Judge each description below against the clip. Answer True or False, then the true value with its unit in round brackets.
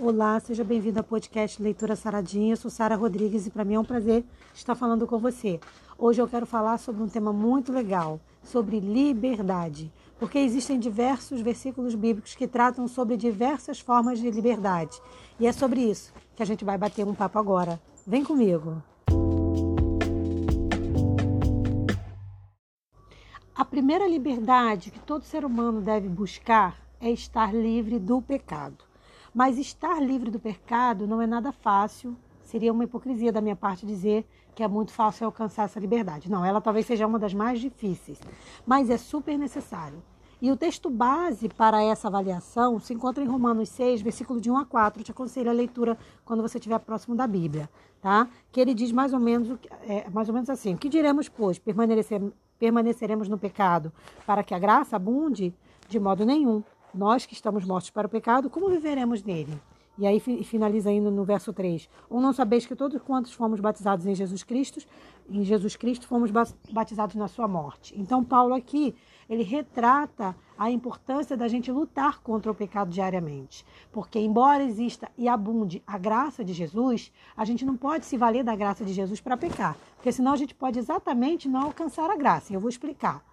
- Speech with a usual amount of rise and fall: True (3.3 semitones)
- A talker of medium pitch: False (230 Hz)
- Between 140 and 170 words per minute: False (180 wpm)